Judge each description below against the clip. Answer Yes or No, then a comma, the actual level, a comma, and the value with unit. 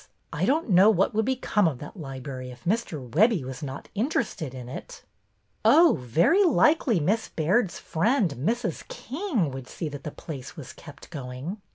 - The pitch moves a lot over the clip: Yes, wide, 8.9 semitones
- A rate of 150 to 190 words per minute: Yes, average, 175 wpm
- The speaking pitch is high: No, medium, 170 Hz